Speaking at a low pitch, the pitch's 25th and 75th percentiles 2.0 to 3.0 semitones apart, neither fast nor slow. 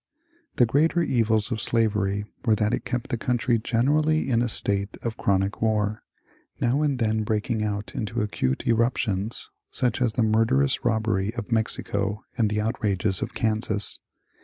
Yes: low, 110 Hz; narrow, 2.5 semitones; average, 160 wpm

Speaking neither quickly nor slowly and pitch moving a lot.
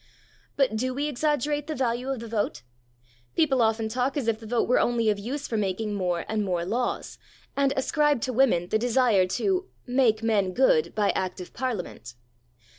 No: average, 190 wpm; average, 4.3 semitones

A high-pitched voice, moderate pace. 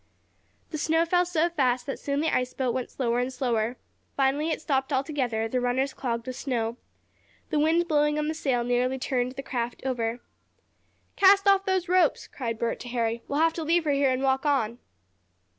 Yes: very high, 265 Hz; average, 195 wpm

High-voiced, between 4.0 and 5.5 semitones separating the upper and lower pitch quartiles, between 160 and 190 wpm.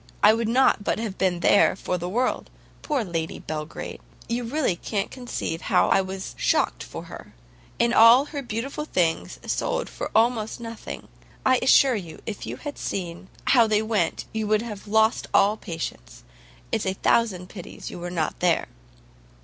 Yes: high, 215 Hz; average, 4.5 semitones; average, 170 wpm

